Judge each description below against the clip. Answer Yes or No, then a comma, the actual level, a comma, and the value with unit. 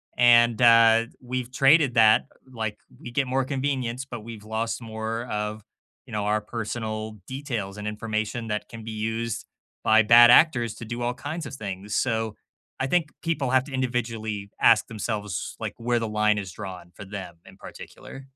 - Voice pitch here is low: Yes, low, 115 Hz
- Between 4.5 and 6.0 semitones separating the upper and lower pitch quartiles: No, narrow, 2.6 semitones